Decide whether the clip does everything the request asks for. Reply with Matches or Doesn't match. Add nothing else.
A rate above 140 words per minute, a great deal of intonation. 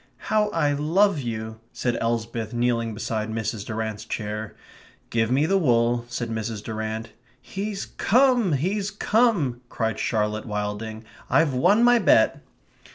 Doesn't match